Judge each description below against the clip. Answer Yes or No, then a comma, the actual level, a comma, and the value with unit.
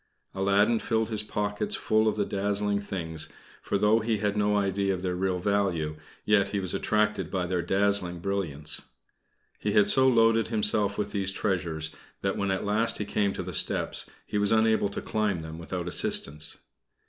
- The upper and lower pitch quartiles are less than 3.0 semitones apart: Yes, narrow, 2.4 semitones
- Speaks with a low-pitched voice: Yes, low, 100 Hz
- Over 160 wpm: Yes, average, 185 wpm